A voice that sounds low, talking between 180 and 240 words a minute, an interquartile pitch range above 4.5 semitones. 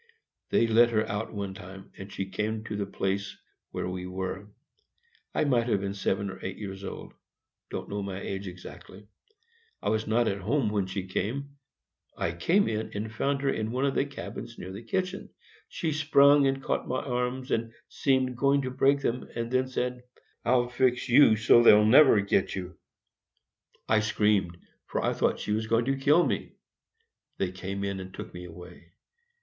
Yes: low, 110 Hz; average, 185 wpm; average, 4.9 semitones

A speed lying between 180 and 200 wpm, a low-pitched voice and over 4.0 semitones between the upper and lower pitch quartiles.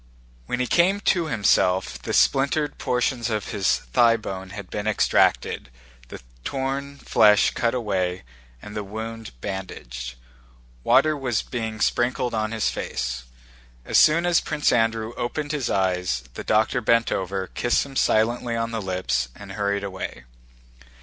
No: average, 145 wpm; low, 110 Hz; average, 4.5 semitones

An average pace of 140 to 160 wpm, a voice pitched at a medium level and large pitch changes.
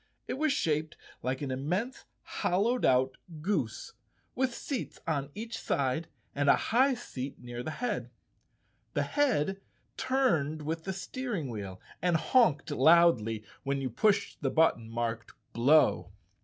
Yes: average, 150 wpm; medium, 155 Hz; wide, 8.7 semitones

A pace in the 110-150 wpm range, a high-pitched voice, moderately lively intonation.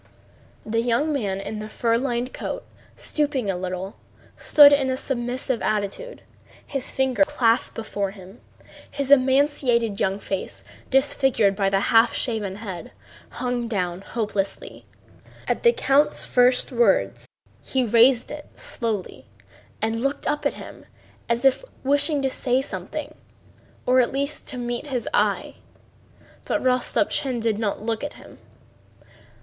Yes: average, 140 wpm; high, 240 Hz; average, 3.9 semitones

